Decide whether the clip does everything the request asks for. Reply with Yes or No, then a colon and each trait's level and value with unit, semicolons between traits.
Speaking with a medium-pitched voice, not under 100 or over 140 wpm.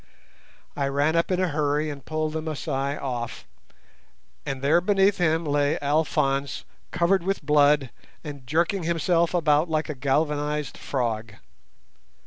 Yes: medium, 150 Hz; slow, 135 wpm